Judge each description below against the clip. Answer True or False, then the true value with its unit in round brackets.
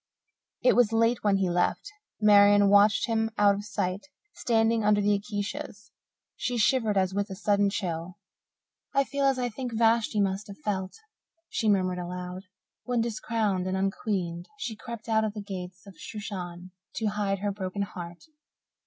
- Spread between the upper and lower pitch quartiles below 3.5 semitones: True (2.8 semitones)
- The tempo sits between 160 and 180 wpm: True (165 wpm)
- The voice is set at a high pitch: True (205 Hz)